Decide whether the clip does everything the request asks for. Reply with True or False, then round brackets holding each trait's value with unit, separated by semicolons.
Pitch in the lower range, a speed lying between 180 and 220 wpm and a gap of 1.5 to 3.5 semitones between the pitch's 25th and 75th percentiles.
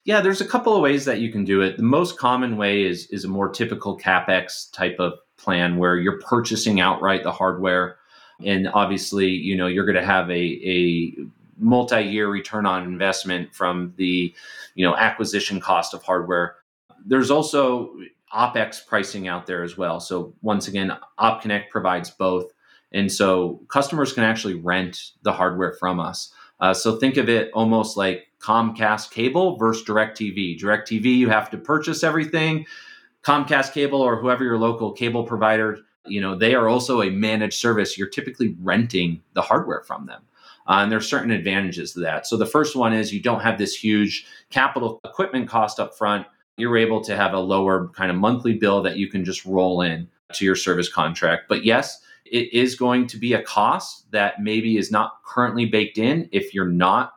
False (105 Hz; 185 wpm; 3.9 semitones)